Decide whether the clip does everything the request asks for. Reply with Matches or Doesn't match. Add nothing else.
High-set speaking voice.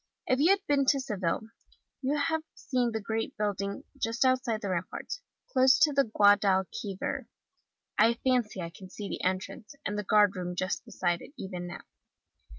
Matches